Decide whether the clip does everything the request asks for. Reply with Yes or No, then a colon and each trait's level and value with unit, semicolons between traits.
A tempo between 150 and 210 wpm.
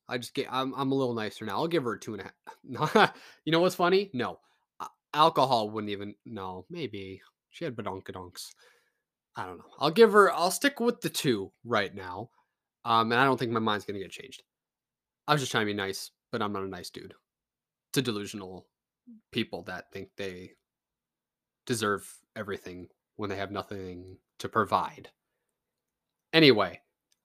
Yes: average, 180 wpm